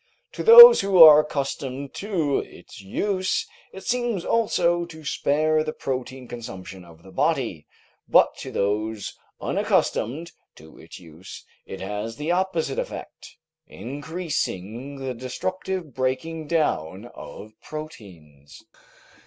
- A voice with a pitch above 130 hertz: Yes, medium, 140 Hz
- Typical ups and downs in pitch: No, wide, 8.1 semitones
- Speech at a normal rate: No, slow, 120 wpm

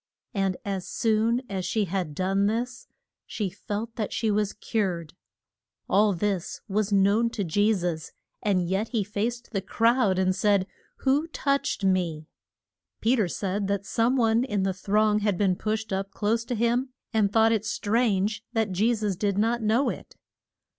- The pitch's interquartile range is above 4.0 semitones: No, average, 2.8 semitones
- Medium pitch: No, high, 210 Hz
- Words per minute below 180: Yes, average, 170 wpm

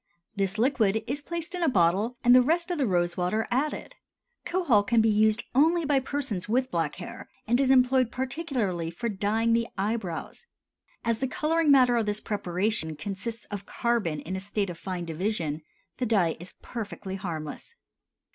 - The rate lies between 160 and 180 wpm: Yes, average, 175 wpm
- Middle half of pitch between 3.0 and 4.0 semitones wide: No, wide, 5.6 semitones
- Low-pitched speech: No, high, 220 Hz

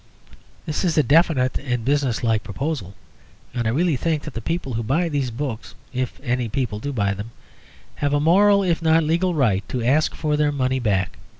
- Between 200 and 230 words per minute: Yes, fast, 205 wpm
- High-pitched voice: No, low, 135 Hz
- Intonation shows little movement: No, average, 5.2 semitones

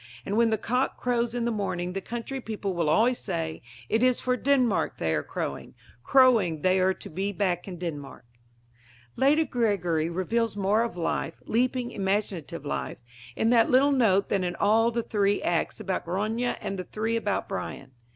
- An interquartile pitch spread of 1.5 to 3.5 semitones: No, average, 4.6 semitones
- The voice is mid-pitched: No, high, 205 Hz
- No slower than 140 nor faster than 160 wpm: No, average, 180 wpm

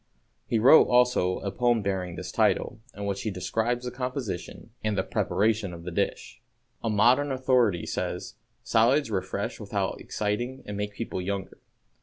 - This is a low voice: Yes, low, 110 Hz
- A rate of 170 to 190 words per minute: No, average, 155 wpm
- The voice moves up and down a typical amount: Yes, average, 3.9 semitones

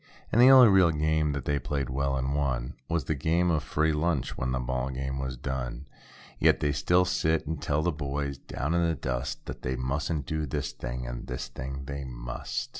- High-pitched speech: No, very low, 70 Hz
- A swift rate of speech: Yes, fast, 215 wpm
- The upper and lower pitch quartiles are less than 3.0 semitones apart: No, average, 3.4 semitones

